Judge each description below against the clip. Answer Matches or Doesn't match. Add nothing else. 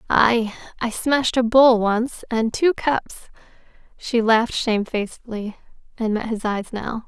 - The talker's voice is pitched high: Matches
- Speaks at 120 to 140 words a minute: Matches